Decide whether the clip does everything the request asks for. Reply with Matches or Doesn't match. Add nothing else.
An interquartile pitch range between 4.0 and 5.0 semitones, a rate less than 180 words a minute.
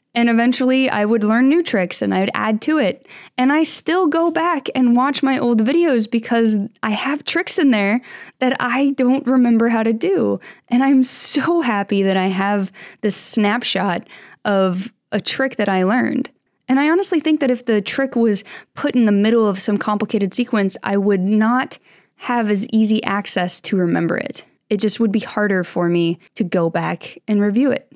Doesn't match